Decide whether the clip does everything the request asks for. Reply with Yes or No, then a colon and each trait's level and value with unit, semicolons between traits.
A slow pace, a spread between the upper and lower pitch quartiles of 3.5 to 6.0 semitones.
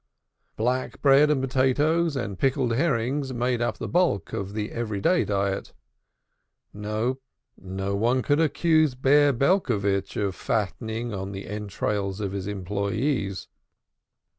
Yes: slow, 130 wpm; average, 5.2 semitones